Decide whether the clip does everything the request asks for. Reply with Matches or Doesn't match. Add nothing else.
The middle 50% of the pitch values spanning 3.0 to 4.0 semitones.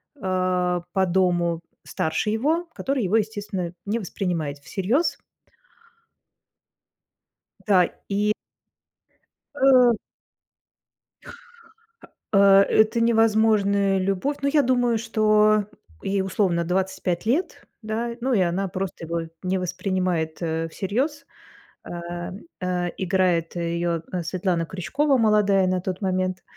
Matches